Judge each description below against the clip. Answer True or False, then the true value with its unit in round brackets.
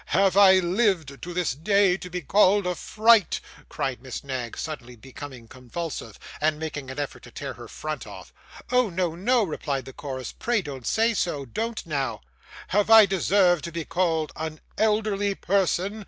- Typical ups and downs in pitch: False (6.1 semitones)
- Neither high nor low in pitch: True (175 Hz)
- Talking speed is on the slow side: False (175 wpm)